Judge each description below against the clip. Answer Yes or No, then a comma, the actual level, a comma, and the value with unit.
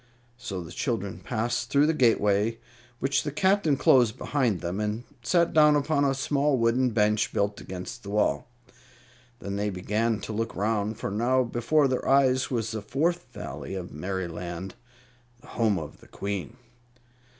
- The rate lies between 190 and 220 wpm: No, average, 160 wpm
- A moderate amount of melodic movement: Yes, average, 4.7 semitones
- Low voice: Yes, low, 115 Hz